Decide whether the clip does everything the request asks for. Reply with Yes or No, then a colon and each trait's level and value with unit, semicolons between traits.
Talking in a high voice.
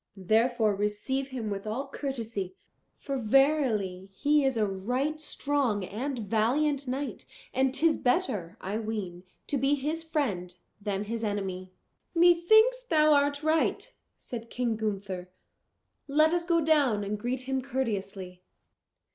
Yes: high, 245 Hz